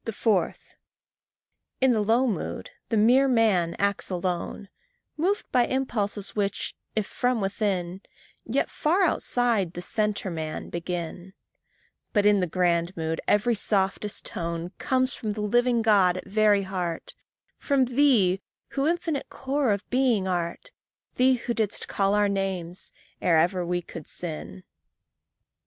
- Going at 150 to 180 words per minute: No, average, 140 wpm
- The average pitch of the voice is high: Yes, high, 205 Hz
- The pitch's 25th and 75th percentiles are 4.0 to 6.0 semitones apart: Yes, average, 5.2 semitones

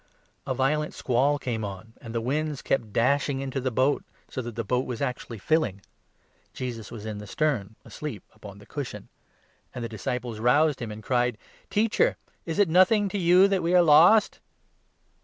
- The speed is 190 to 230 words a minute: Yes, average, 195 wpm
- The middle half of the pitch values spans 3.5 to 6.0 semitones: Yes, average, 5.3 semitones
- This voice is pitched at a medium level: No, low, 130 Hz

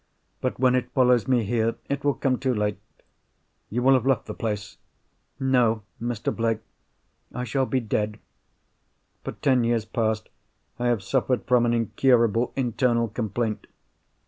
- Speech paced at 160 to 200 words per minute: No, average, 145 wpm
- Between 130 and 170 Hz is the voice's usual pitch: No, low, 120 Hz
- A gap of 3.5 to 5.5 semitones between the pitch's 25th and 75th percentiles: No, narrow, 2.4 semitones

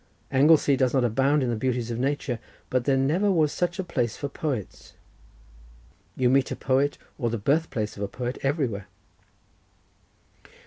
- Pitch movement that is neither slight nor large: Yes, average, 3.1 semitones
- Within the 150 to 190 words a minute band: Yes, average, 170 wpm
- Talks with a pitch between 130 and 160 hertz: Yes, low, 135 Hz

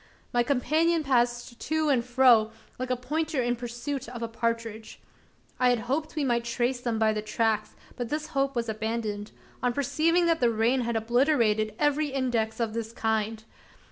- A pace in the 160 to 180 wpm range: Yes, average, 175 wpm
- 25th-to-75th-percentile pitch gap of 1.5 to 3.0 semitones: No, average, 3.4 semitones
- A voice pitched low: No, high, 240 Hz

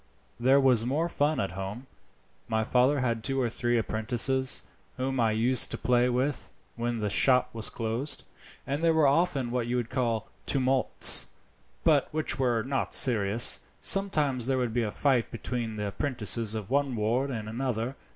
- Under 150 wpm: No, average, 170 wpm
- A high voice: No, low, 125 Hz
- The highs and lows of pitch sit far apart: No, average, 3.0 semitones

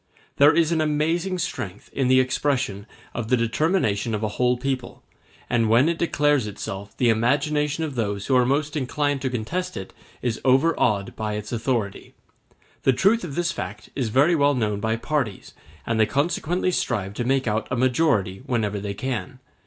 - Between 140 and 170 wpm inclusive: No, average, 180 wpm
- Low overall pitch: Yes, low, 130 Hz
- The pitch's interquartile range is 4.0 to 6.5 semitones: Yes, average, 5.2 semitones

